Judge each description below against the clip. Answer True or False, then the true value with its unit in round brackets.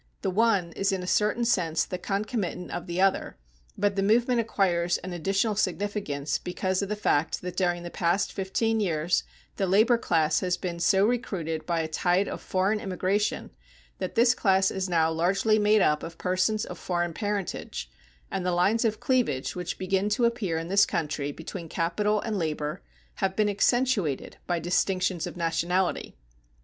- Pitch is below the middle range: False (185 Hz)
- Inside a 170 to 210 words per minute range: True (175 wpm)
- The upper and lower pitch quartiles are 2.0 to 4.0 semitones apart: True (3.3 semitones)